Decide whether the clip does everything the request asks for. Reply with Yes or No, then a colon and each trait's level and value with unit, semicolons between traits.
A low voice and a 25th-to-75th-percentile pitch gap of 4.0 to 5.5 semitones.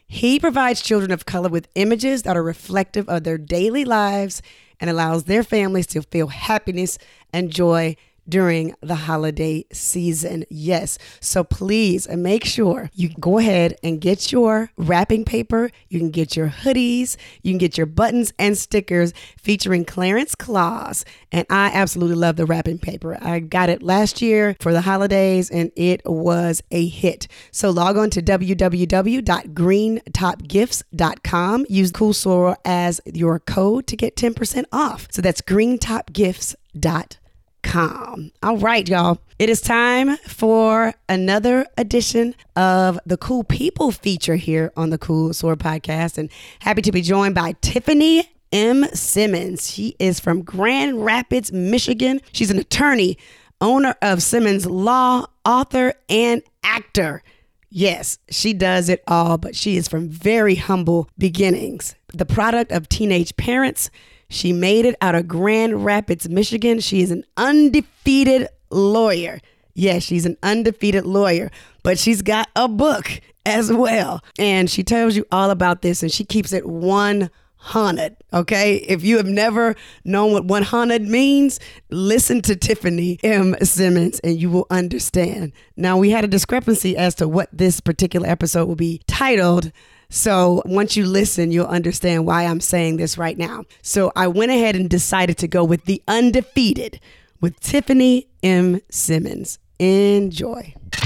No: high, 190 Hz; average, 4.3 semitones